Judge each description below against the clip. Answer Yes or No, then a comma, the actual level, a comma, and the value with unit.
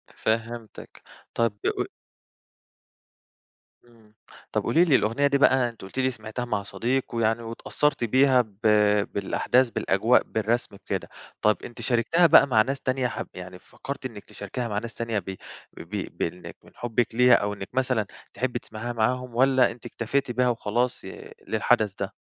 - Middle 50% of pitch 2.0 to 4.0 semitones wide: Yes, average, 2.9 semitones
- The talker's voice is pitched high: No, low, 120 Hz